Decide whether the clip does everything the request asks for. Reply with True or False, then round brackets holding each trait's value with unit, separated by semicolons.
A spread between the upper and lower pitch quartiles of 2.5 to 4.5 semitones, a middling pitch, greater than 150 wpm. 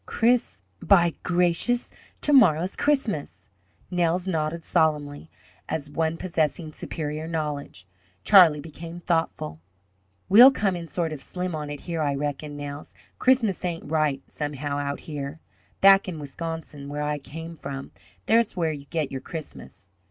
False (3.3 semitones; 160 Hz; 145 wpm)